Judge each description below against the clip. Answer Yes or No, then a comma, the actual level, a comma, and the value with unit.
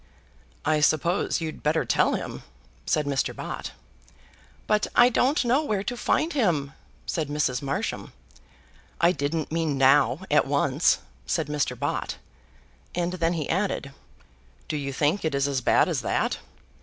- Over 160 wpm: No, average, 150 wpm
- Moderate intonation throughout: Yes, average, 5.0 semitones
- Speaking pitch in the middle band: Yes, medium, 155 Hz